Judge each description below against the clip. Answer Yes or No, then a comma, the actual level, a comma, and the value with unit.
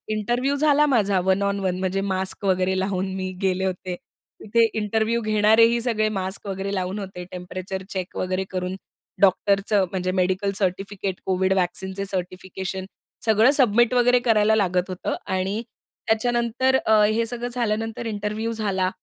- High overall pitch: Yes, high, 200 Hz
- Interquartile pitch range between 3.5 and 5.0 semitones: No, average, 3.0 semitones